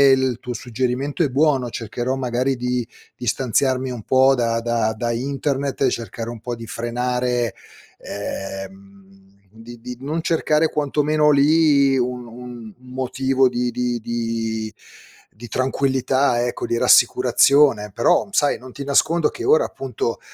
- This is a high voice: No, low, 125 Hz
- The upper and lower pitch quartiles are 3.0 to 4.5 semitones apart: No, narrow, 2.6 semitones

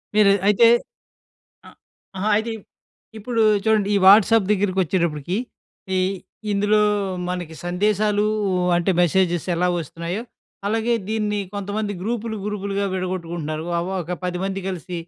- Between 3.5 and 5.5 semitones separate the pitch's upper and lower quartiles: No, average, 3.0 semitones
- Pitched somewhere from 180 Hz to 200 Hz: Yes, high, 195 Hz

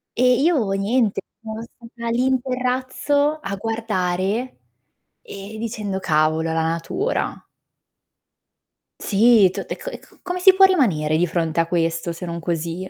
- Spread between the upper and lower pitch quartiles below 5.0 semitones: No, wide, 6.9 semitones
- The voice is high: Yes, high, 215 Hz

